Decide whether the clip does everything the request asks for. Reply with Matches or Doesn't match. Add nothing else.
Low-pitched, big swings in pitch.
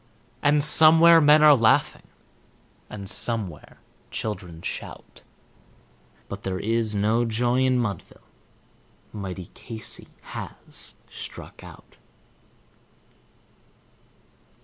Matches